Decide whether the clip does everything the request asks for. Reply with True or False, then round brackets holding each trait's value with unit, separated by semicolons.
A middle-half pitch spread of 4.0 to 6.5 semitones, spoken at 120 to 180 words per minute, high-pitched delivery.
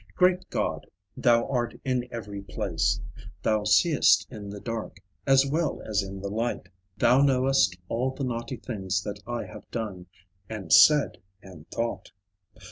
False (4.4 semitones; 150 wpm; 115 Hz)